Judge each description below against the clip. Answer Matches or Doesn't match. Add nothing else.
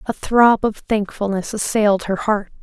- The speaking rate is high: Doesn't match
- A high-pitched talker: Matches